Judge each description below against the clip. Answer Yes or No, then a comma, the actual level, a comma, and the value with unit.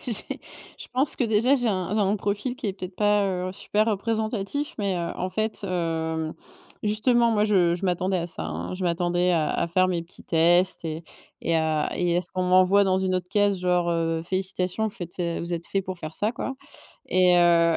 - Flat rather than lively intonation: No, average, 3.3 semitones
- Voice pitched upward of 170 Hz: Yes, medium, 185 Hz